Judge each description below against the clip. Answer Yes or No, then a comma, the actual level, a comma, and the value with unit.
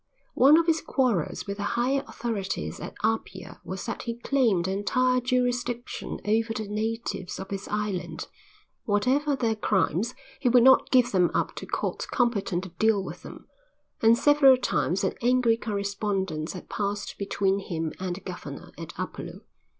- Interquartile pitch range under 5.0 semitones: Yes, average, 4.1 semitones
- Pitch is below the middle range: No, high, 215 Hz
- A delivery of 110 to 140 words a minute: No, average, 160 wpm